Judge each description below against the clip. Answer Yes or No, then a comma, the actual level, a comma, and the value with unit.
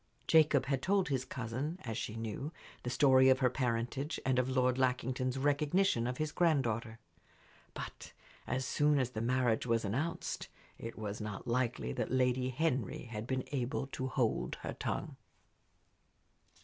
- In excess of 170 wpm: No, average, 155 wpm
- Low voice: Yes, low, 130 Hz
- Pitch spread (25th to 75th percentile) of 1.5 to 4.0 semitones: Yes, average, 3.0 semitones